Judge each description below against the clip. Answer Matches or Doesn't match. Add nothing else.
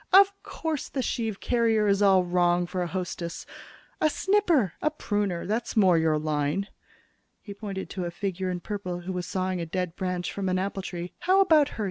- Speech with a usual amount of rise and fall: Matches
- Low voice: Doesn't match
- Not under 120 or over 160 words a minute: Doesn't match